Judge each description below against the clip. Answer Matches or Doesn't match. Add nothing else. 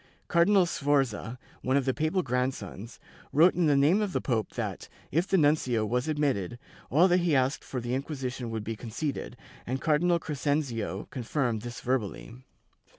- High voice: Doesn't match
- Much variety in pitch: Doesn't match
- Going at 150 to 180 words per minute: Matches